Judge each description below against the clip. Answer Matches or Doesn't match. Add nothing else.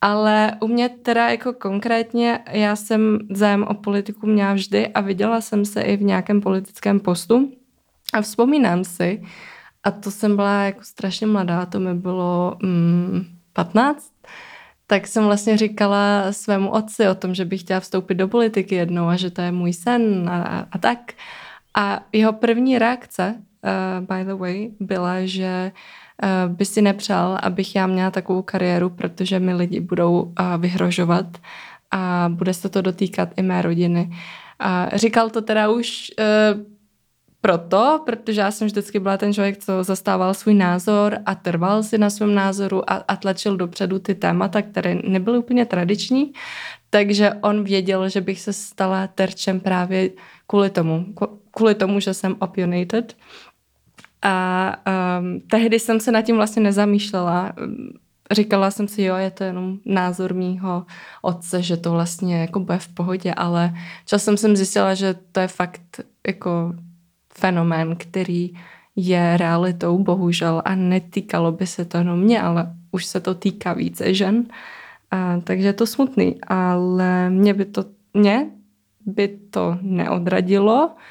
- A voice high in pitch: Matches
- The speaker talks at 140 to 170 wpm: Matches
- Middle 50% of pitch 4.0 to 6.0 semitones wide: Doesn't match